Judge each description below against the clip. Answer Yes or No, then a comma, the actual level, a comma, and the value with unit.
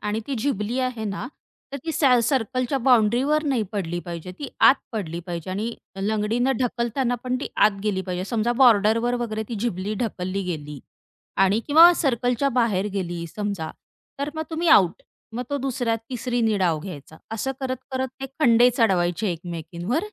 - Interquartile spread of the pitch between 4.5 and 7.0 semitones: Yes, average, 5.1 semitones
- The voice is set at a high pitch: Yes, high, 225 Hz